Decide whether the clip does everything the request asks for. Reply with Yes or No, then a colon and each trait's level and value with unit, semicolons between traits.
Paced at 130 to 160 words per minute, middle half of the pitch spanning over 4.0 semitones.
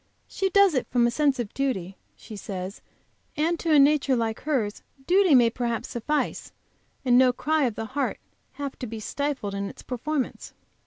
No: average, 180 wpm; average, 4.7 semitones